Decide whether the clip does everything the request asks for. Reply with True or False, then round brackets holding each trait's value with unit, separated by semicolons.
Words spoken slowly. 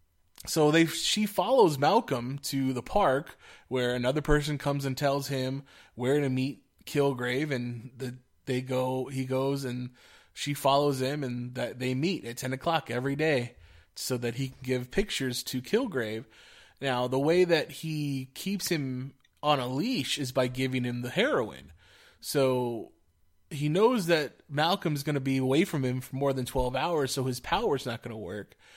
False (180 wpm)